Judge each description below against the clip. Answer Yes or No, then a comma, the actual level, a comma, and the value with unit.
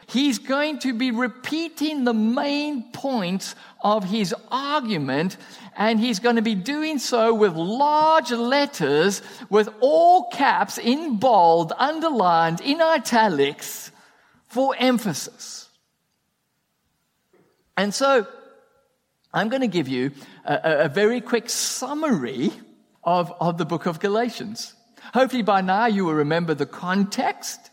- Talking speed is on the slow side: Yes, slow, 125 wpm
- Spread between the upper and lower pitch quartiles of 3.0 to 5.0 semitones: No, wide, 5.6 semitones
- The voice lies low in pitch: No, high, 235 Hz